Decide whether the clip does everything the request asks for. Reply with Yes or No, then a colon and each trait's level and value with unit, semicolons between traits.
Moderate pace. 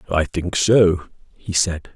Yes: average, 155 wpm